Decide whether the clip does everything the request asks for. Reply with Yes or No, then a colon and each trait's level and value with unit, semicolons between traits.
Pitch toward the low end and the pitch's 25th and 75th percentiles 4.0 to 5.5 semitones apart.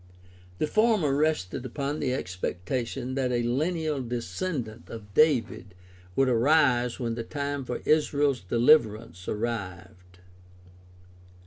Yes: low, 125 Hz; average, 4.8 semitones